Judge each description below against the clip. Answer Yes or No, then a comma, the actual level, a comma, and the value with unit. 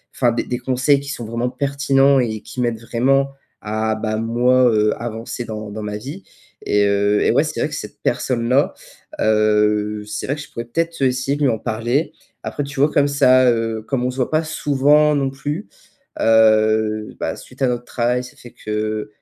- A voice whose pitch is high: No, low, 120 Hz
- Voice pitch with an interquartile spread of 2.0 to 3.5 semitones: No, average, 4.0 semitones